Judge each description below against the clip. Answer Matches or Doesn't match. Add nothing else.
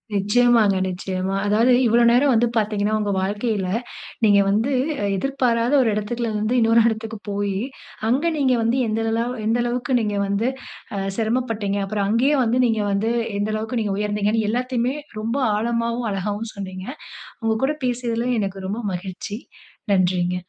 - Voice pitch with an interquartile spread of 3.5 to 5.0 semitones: Doesn't match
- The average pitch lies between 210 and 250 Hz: Matches